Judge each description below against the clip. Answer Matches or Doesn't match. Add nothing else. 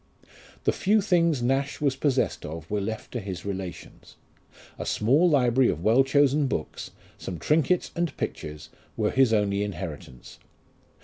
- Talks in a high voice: Doesn't match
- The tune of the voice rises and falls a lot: Matches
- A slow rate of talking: Doesn't match